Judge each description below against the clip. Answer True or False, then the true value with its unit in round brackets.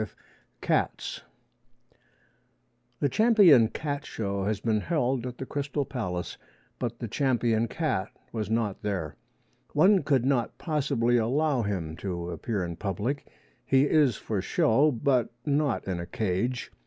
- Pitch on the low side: True (120 Hz)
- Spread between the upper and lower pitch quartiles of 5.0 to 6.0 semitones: True (5.6 semitones)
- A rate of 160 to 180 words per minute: False (140 wpm)